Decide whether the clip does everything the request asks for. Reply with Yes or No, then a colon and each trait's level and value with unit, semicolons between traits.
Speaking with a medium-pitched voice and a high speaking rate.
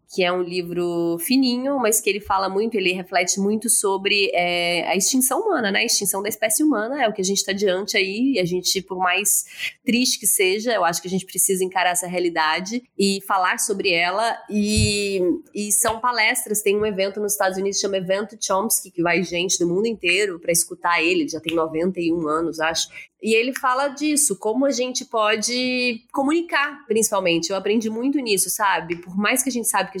No: high, 200 Hz; fast, 205 wpm